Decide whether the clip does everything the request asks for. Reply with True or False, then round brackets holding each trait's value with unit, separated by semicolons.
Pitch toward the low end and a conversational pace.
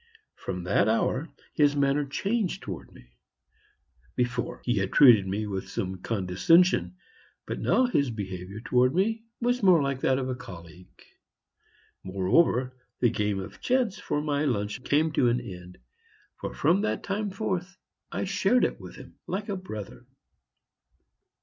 True (130 Hz; 150 wpm)